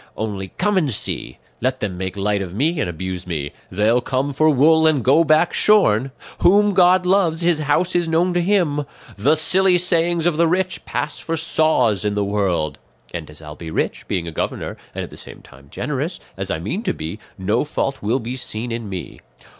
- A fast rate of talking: Yes, fast, 210 wpm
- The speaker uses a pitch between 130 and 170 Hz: Yes, low, 135 Hz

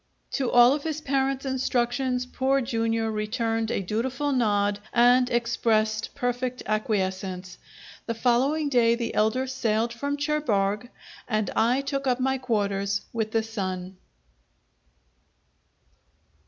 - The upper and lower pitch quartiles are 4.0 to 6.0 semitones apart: No, average, 3.4 semitones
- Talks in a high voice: Yes, high, 235 Hz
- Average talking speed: No, slow, 120 wpm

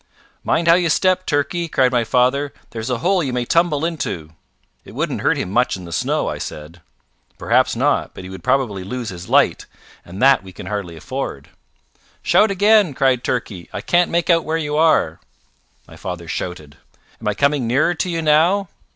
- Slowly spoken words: No, average, 195 wpm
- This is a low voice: Yes, low, 130 Hz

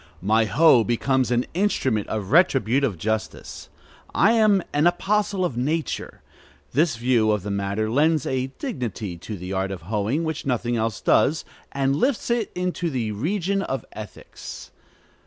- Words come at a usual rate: Yes, average, 155 wpm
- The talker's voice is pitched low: Yes, low, 130 Hz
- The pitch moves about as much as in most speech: No, wide, 7.5 semitones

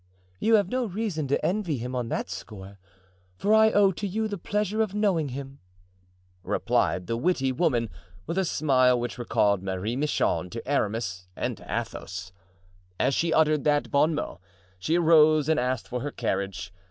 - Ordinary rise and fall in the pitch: No, wide, 7.6 semitones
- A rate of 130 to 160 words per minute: No, average, 175 wpm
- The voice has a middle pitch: Yes, medium, 145 Hz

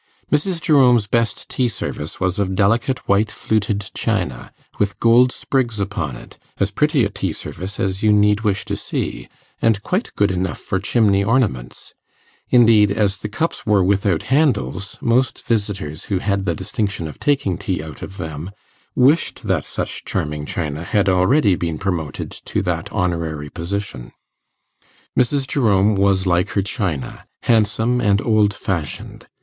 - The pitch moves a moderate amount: Yes, average, 3.9 semitones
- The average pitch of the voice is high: No, low, 100 Hz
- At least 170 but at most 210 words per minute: No, average, 155 wpm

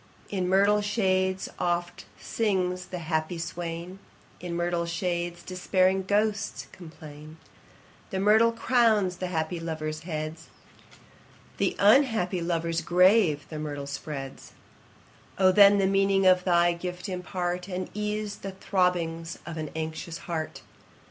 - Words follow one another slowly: Yes, slow, 125 wpm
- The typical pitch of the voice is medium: Yes, medium, 180 Hz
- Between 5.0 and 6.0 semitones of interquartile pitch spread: No, narrow, 2.6 semitones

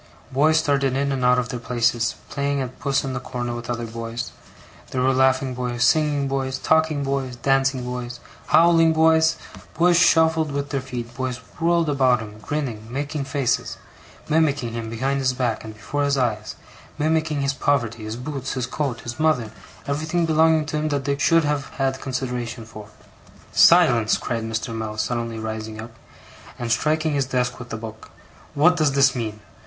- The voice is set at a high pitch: No, low, 130 Hz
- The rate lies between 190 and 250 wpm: No, average, 180 wpm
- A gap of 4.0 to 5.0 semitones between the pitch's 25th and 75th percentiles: No, average, 3.6 semitones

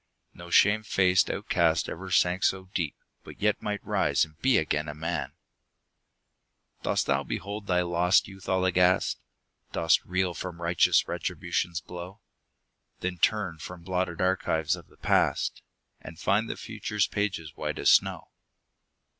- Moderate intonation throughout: No, narrow, 2.3 semitones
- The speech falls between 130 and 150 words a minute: Yes, average, 145 wpm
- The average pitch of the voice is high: No, very low, 90 Hz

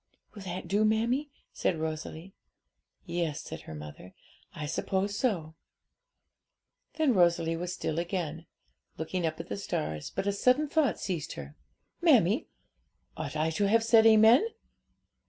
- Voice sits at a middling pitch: Yes, medium, 180 Hz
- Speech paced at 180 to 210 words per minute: No, slow, 135 wpm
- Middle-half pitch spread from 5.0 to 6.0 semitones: Yes, wide, 5.4 semitones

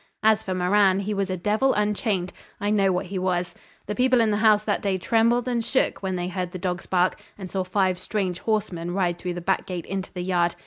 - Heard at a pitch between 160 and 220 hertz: Yes, high, 190 Hz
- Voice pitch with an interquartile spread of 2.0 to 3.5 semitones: Yes, narrow, 2.6 semitones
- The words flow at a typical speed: No, fast, 235 wpm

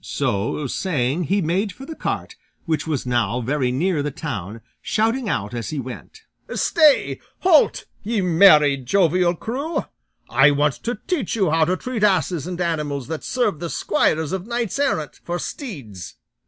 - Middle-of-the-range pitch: Yes, medium, 170 Hz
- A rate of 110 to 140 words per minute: No, average, 165 wpm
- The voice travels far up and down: Yes, wide, 6.8 semitones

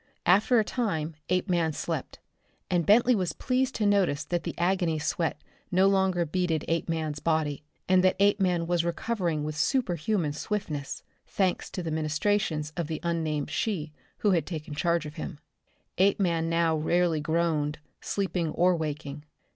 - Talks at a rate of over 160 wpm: No, average, 150 wpm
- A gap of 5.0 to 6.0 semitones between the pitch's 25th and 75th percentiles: No, average, 3.3 semitones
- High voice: No, medium, 170 Hz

